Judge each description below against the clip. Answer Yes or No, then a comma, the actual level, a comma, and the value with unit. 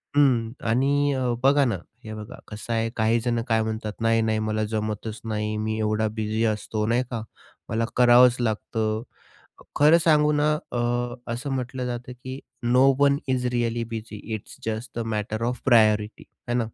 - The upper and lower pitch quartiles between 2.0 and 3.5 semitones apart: Yes, narrow, 2.5 semitones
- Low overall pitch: Yes, low, 115 Hz